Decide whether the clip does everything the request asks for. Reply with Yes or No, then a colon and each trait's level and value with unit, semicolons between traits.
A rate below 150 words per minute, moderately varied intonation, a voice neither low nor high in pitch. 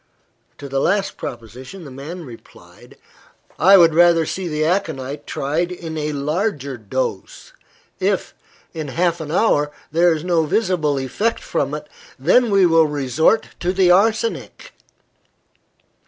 Yes: average, 140 wpm; average, 4.2 semitones; medium, 160 Hz